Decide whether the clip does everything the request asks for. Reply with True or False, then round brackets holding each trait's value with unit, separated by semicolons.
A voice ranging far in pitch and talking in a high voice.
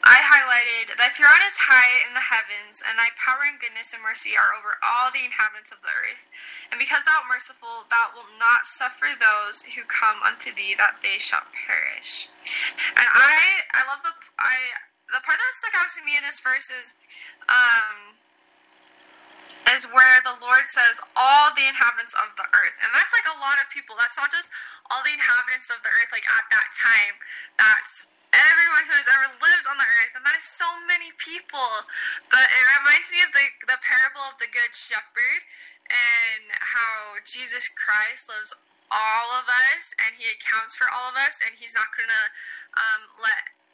True (5.9 semitones; 260 Hz)